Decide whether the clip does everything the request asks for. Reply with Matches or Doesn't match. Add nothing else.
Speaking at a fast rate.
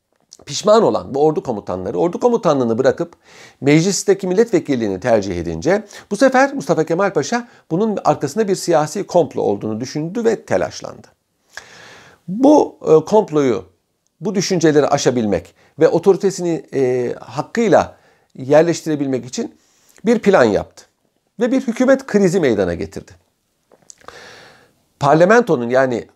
Doesn't match